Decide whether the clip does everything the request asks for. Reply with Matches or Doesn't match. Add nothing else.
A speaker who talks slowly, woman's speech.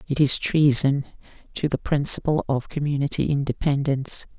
Matches